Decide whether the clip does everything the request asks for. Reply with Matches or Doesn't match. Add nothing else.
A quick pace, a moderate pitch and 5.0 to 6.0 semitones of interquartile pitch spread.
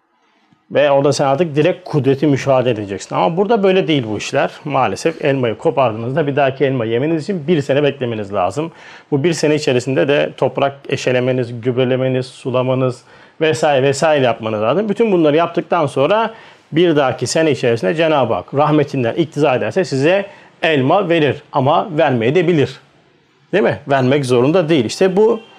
Doesn't match